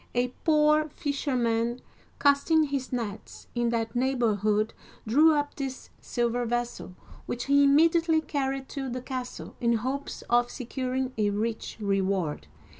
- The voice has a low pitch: No, very high, 250 Hz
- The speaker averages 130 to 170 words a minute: Yes, slow, 135 wpm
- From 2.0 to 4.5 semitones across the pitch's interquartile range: Yes, average, 3.5 semitones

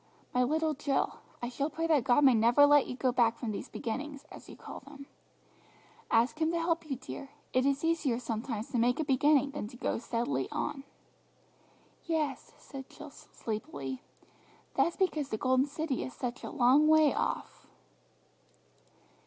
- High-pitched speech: Yes, very high, 275 Hz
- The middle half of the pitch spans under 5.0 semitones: Yes, average, 3.7 semitones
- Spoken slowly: No, average, 170 wpm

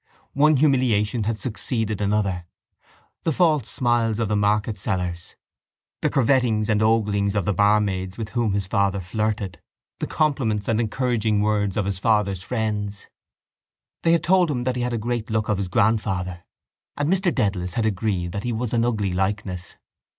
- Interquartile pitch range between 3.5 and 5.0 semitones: No, average, 3.1 semitones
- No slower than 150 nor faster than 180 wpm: Yes, average, 165 wpm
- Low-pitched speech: Yes, low, 105 Hz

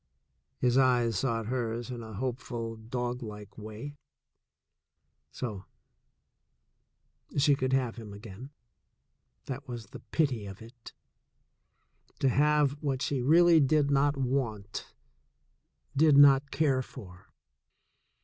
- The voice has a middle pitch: No, low, 125 Hz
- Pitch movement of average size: Yes, average, 3.7 semitones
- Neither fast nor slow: No, slow, 115 wpm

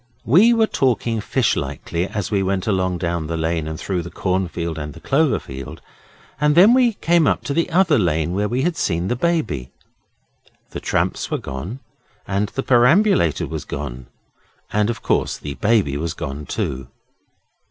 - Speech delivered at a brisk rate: No, average, 165 wpm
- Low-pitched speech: Yes, low, 100 Hz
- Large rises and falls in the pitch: Yes, wide, 8.9 semitones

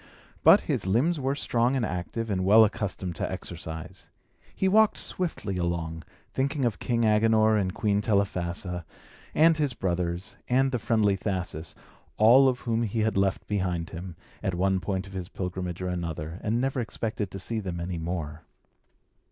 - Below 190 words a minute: Yes, average, 170 wpm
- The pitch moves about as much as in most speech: Yes, average, 4.5 semitones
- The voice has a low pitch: Yes, low, 100 Hz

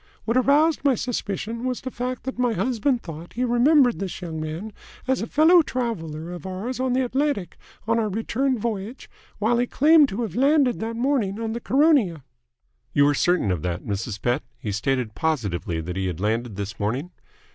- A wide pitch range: Yes, wide, 8.6 semitones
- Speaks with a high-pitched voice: Yes, high, 220 Hz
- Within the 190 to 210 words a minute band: Yes, average, 195 wpm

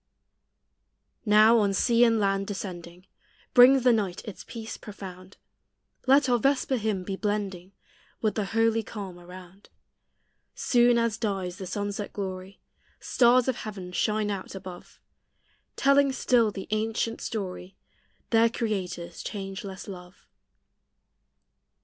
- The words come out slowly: Yes, slow, 120 wpm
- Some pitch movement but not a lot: Yes, average, 3.3 semitones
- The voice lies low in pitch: No, high, 205 Hz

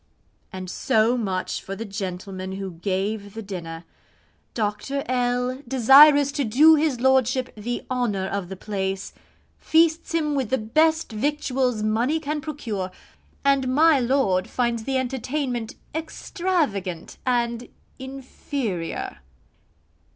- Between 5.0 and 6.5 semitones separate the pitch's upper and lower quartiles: Yes, wide, 5.6 semitones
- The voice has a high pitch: Yes, high, 245 Hz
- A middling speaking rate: No, slow, 120 wpm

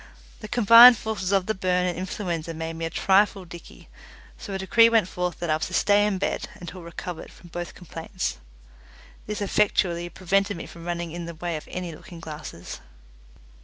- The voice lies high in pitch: No, medium, 180 Hz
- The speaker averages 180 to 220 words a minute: Yes, average, 190 wpm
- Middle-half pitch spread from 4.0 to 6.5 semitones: No, average, 2.8 semitones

